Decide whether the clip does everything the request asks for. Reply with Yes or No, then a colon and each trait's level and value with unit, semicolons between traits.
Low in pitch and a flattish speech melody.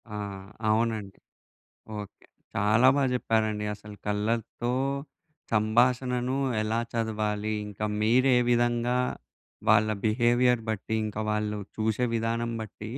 Yes: low, 110 Hz; narrow, 2.1 semitones